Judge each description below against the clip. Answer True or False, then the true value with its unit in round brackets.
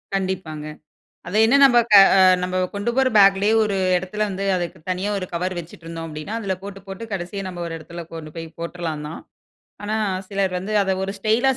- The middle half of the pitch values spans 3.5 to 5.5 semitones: False (3.0 semitones)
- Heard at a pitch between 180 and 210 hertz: True (190 Hz)